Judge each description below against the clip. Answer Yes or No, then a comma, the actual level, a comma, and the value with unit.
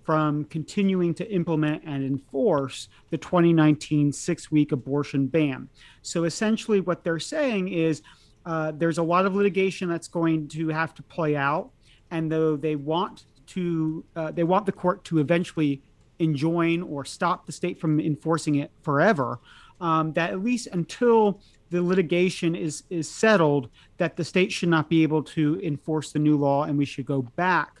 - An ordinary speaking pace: Yes, average, 170 wpm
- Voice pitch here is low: No, medium, 160 Hz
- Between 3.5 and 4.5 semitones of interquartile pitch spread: No, average, 2.9 semitones